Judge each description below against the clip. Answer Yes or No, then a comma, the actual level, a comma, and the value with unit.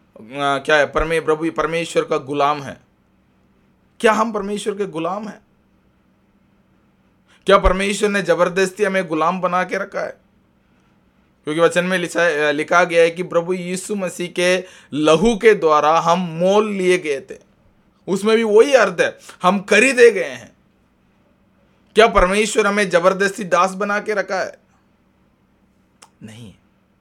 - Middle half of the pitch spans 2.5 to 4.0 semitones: No, average, 4.6 semitones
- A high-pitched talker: No, medium, 180 Hz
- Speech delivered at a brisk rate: No, average, 145 wpm